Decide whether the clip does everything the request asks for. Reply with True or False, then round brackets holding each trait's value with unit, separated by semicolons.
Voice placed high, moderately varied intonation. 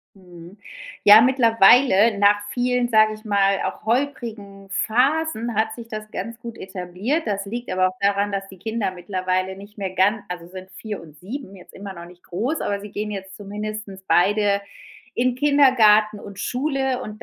True (205 Hz; 3.2 semitones)